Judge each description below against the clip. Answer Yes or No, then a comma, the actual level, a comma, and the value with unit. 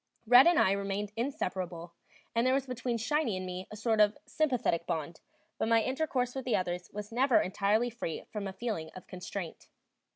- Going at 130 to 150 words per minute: No, average, 190 wpm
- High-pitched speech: Yes, high, 215 Hz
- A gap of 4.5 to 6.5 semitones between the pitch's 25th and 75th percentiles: Yes, average, 5.1 semitones